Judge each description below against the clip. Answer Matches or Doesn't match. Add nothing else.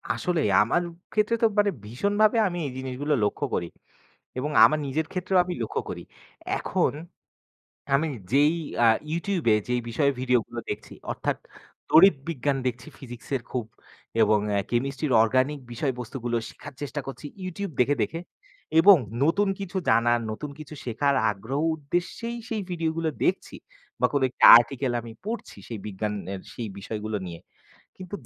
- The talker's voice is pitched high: Doesn't match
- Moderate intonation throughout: Doesn't match